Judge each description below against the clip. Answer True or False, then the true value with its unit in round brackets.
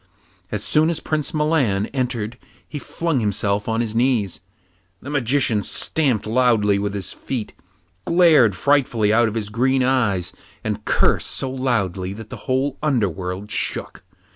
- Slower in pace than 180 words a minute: True (145 wpm)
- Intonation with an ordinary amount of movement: True (4.7 semitones)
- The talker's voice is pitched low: True (120 Hz)